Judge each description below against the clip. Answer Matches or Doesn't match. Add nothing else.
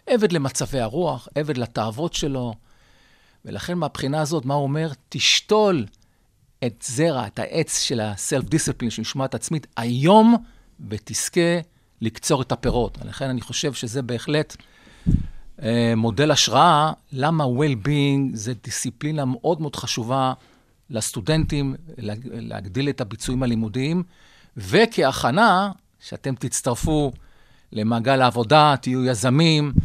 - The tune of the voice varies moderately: Matches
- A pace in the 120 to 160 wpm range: Doesn't match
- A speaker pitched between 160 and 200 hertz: Doesn't match